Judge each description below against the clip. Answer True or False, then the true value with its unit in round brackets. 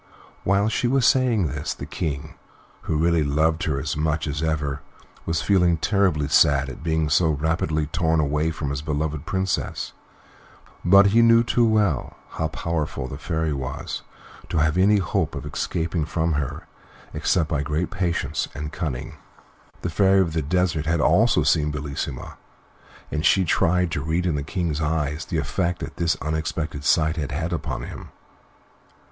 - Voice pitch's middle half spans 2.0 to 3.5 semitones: True (2.9 semitones)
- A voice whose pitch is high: False (80 Hz)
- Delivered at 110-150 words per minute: False (165 wpm)